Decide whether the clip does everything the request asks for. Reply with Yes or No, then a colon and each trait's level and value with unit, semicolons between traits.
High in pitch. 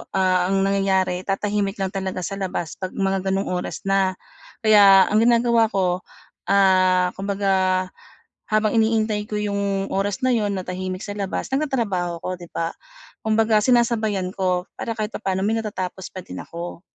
Yes: high, 195 Hz